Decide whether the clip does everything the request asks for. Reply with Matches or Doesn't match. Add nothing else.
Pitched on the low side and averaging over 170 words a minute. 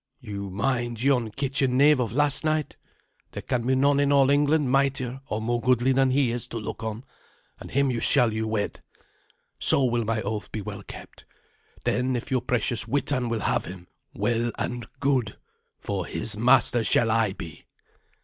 Matches